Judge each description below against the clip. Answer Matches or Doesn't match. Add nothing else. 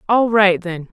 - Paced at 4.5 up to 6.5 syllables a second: Doesn't match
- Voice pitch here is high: Matches